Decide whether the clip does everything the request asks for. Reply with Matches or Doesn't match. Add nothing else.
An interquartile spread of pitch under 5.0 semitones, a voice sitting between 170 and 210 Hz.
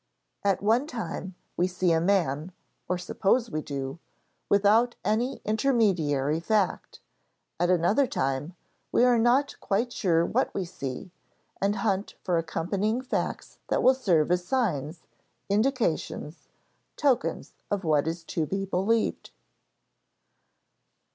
Doesn't match